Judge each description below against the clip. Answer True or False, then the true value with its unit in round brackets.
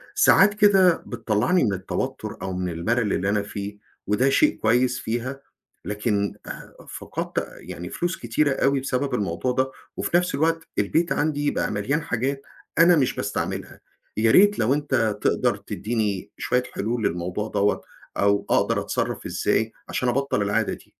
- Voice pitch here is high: False (120 Hz)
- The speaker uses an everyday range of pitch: False (5.9 semitones)